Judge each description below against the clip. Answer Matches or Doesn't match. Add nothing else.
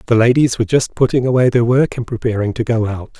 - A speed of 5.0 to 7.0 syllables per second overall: Matches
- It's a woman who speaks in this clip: Doesn't match